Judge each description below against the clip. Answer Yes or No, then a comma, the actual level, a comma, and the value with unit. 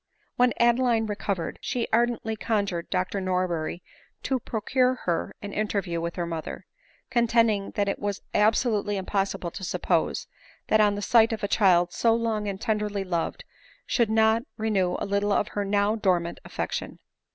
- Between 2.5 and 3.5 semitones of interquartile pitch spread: Yes, average, 2.9 semitones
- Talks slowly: No, average, 155 wpm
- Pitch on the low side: No, high, 205 Hz